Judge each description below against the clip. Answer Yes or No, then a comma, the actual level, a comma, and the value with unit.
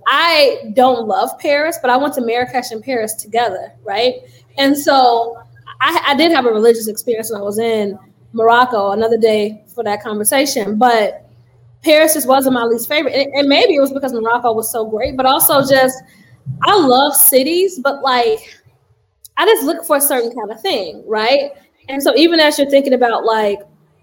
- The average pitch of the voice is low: No, high, 245 Hz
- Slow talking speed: No, average, 185 wpm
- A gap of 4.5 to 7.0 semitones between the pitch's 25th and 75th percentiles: No, average, 4.0 semitones